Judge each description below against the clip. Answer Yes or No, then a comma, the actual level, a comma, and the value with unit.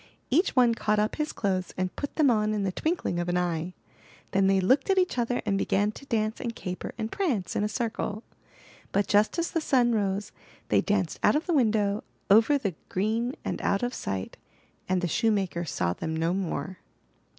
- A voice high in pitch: Yes, high, 210 Hz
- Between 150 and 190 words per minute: No, fast, 205 wpm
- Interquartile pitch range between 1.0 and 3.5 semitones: No, average, 4.5 semitones